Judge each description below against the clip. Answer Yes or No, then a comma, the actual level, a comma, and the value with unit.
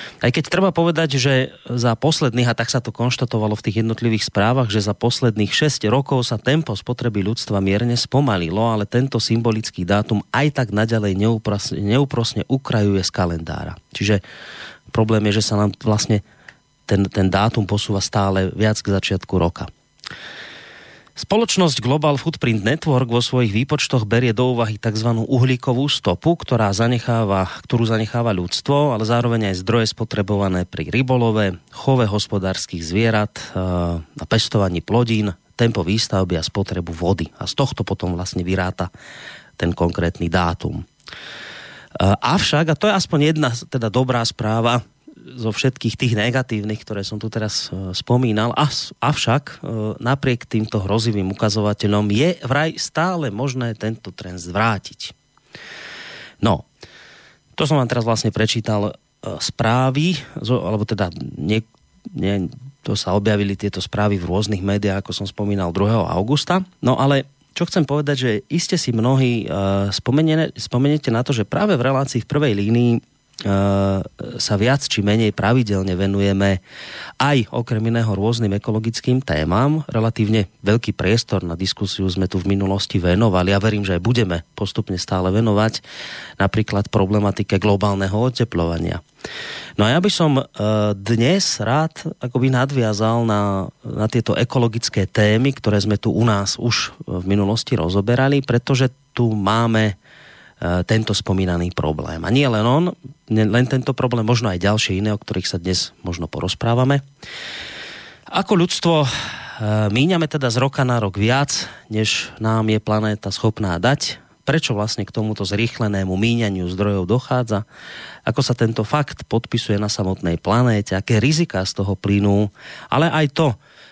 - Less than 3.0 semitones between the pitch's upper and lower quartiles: No, average, 4.1 semitones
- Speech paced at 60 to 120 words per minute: No, average, 140 wpm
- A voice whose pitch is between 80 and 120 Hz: Yes, low, 110 Hz